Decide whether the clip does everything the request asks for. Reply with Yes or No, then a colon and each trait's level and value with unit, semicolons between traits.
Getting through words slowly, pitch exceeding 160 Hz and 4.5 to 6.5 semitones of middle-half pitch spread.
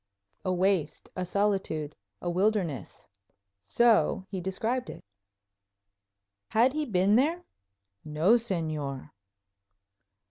Yes: slow, 95 wpm; high, 190 Hz; wide, 5.5 semitones